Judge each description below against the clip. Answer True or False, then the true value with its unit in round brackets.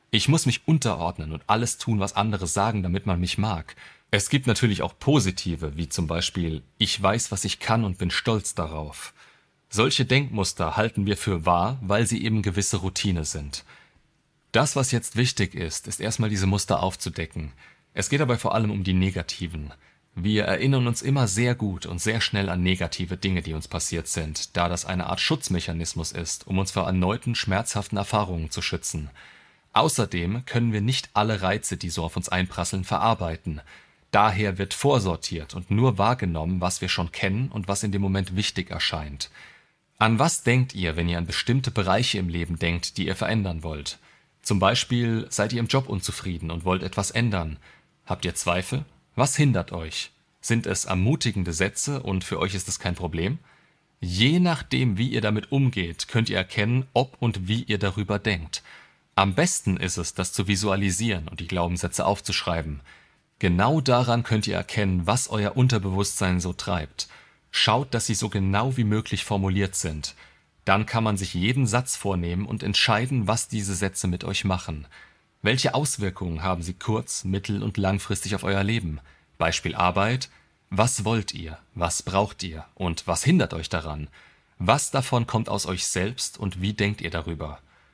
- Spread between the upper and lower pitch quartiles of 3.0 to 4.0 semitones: False (4.5 semitones)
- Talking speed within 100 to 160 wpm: False (175 wpm)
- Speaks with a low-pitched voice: True (100 Hz)